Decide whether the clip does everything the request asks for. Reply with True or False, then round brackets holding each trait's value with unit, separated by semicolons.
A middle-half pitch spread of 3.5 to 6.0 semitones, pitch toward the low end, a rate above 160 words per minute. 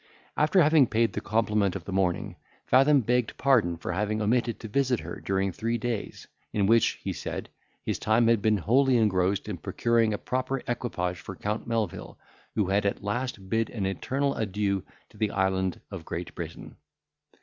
True (3.8 semitones; 110 Hz; 180 wpm)